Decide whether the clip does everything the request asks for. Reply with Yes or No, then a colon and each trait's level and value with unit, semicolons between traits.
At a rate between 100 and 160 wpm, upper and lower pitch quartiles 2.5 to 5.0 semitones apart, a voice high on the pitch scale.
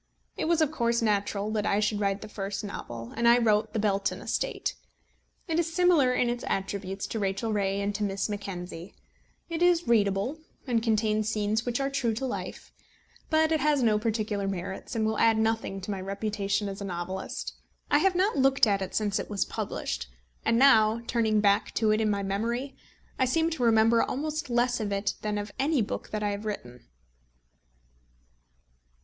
No: average, 190 wpm; average, 3.5 semitones; high, 215 Hz